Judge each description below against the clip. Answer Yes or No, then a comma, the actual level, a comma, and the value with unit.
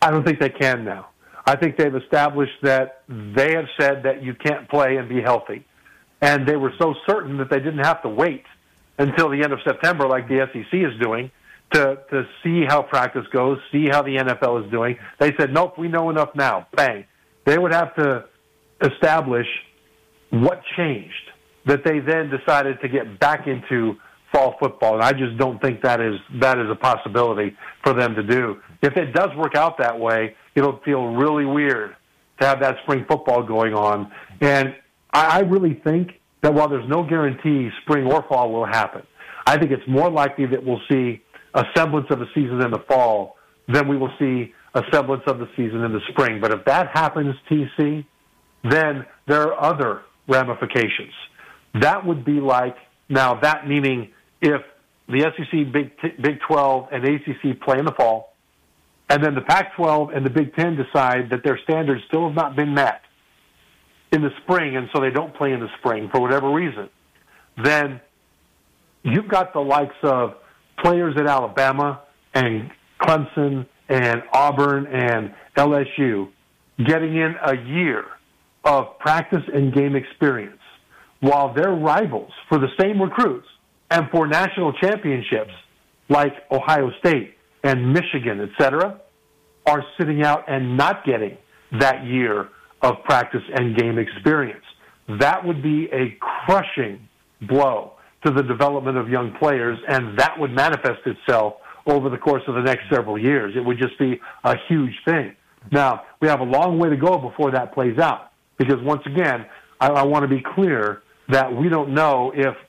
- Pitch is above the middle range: No, medium, 140 Hz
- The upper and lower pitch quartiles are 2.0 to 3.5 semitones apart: Yes, average, 3.2 semitones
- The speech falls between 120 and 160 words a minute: No, average, 175 wpm